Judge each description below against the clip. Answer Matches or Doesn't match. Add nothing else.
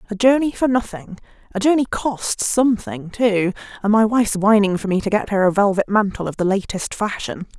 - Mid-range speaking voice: Doesn't match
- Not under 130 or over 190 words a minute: Doesn't match